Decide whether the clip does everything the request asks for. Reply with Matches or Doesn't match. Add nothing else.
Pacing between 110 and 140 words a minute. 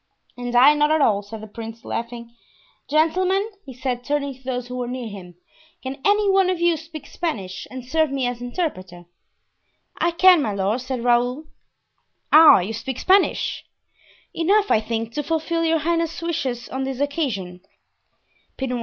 Doesn't match